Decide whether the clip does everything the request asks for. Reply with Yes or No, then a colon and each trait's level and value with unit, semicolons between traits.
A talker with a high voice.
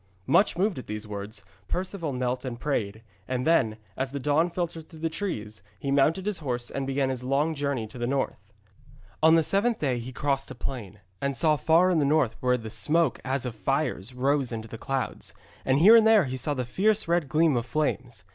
No: low, 135 Hz